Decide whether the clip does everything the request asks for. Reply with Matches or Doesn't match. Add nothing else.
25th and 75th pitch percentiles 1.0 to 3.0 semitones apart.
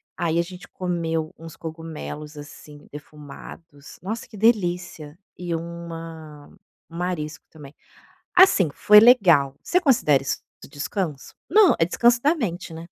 Doesn't match